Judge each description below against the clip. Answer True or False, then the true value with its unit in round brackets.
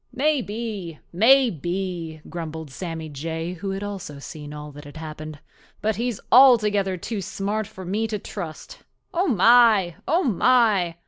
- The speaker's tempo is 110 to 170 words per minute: True (140 wpm)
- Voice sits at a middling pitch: False (195 Hz)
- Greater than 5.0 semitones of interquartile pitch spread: True (5.6 semitones)